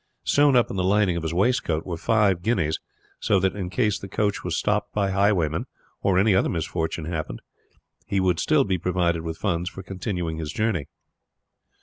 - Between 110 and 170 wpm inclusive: No, average, 190 wpm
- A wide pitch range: No, average, 3.6 semitones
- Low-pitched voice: Yes, very low, 95 Hz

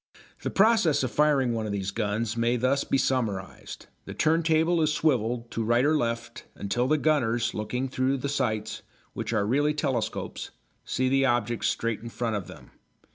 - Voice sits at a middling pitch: No, low, 120 Hz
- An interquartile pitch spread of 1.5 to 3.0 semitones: No, average, 3.9 semitones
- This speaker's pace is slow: No, average, 180 wpm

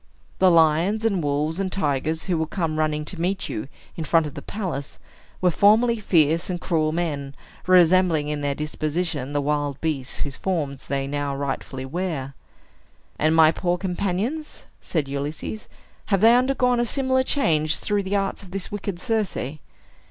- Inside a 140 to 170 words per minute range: Yes, average, 165 wpm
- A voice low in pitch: No, medium, 165 Hz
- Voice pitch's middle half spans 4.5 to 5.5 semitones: Yes, average, 4.9 semitones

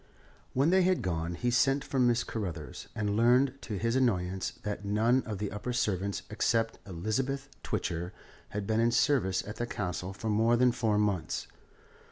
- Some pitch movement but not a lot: Yes, average, 3.7 semitones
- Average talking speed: Yes, average, 175 wpm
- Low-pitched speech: Yes, low, 110 Hz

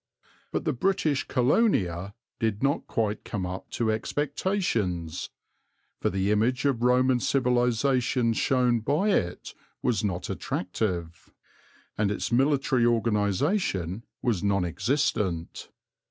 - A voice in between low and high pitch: No, low, 115 Hz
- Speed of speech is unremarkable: No, slow, 110 wpm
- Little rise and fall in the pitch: No, average, 5.3 semitones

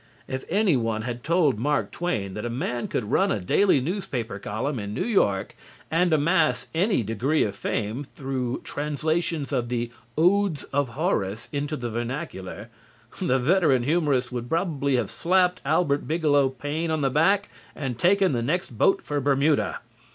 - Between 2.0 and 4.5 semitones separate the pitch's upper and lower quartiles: No, wide, 5.6 semitones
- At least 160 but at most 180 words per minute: Yes, average, 165 wpm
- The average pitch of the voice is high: No, medium, 140 Hz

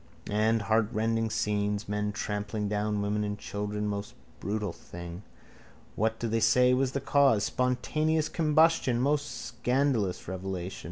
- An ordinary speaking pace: No, slow, 130 wpm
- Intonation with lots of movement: No, average, 3.6 semitones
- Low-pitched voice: Yes, low, 110 Hz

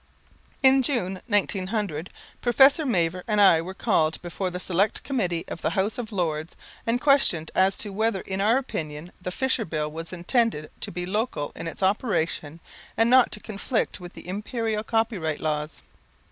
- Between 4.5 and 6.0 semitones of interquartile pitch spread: Yes, average, 5.2 semitones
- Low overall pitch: No, high, 195 Hz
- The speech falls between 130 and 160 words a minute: No, average, 170 wpm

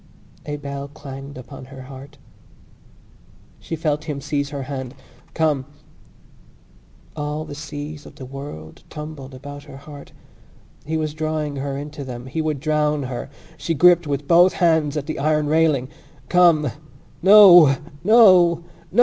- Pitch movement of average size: No, narrow, 2.2 semitones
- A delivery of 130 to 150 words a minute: Yes, average, 145 wpm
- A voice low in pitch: No, medium, 145 Hz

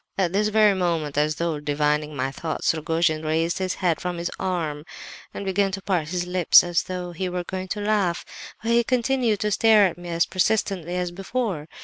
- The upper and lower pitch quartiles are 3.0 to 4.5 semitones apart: Yes, average, 3.4 semitones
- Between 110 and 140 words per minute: No, average, 200 wpm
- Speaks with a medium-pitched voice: Yes, medium, 180 Hz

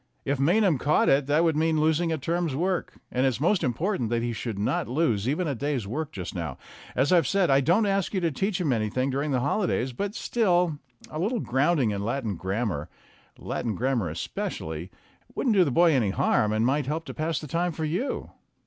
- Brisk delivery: Yes, fast, 215 wpm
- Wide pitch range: Yes, wide, 6.2 semitones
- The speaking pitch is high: No, medium, 145 Hz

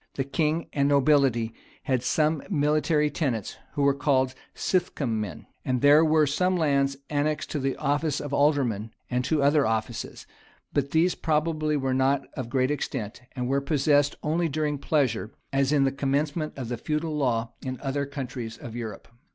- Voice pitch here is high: No, medium, 140 Hz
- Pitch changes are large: No, average, 2.7 semitones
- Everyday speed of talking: Yes, average, 170 wpm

